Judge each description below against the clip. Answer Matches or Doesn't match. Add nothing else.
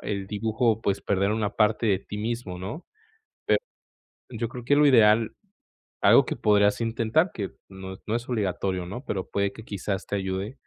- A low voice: Matches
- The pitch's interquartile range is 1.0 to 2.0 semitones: Doesn't match